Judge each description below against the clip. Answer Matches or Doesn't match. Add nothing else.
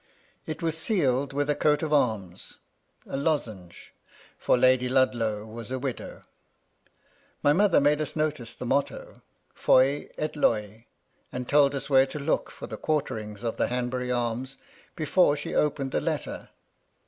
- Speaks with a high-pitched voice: Doesn't match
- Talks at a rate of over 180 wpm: Doesn't match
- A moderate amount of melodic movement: Matches